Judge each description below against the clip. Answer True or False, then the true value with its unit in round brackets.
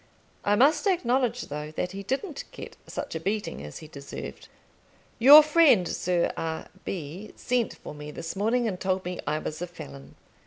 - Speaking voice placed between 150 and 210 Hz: True (190 Hz)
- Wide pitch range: True (7.9 semitones)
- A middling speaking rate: True (180 wpm)